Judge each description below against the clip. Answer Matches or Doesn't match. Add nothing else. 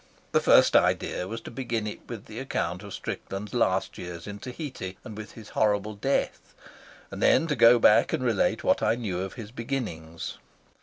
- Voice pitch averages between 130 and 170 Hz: Doesn't match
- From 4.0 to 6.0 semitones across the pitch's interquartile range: Doesn't match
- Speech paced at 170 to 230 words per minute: Matches